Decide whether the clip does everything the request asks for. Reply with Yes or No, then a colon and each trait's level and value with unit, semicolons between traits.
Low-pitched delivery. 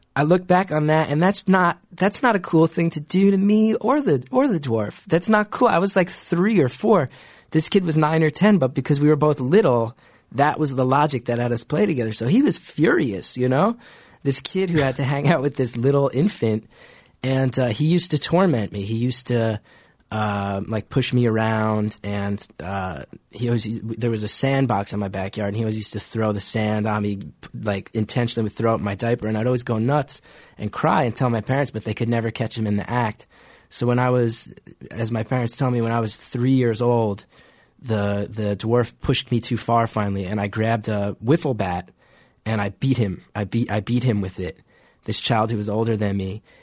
Yes: low, 120 Hz